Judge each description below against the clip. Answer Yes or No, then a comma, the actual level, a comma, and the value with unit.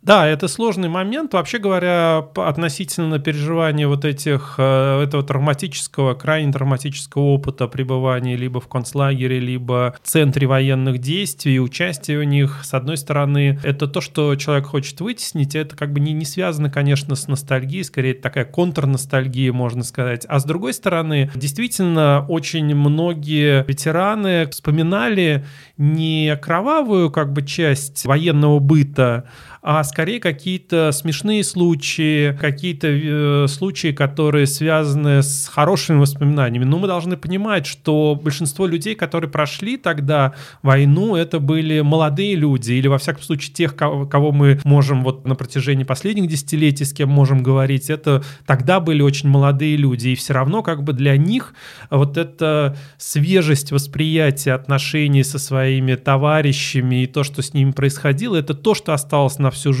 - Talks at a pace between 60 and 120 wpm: No, average, 150 wpm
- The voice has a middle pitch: Yes, medium, 145 Hz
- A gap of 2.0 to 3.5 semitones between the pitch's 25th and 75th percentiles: Yes, average, 2.8 semitones